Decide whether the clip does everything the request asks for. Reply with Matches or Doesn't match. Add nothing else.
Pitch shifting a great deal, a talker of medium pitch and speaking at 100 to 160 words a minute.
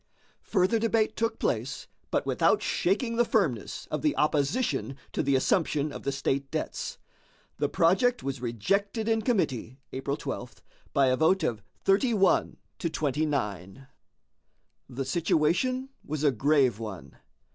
Matches